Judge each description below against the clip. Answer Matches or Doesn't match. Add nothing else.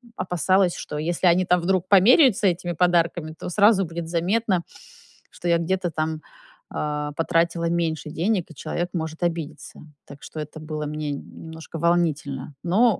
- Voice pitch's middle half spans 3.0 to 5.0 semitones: Doesn't match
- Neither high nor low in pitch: Matches